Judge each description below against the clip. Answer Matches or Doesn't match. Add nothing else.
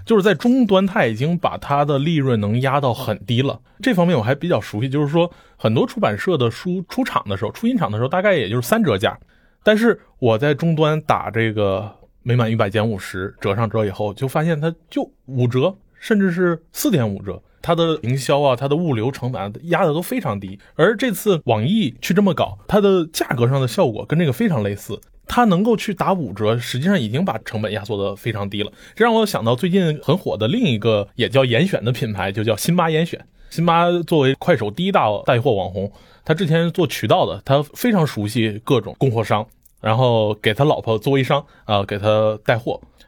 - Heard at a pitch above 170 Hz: Doesn't match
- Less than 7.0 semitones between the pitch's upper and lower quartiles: Doesn't match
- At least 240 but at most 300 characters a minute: Doesn't match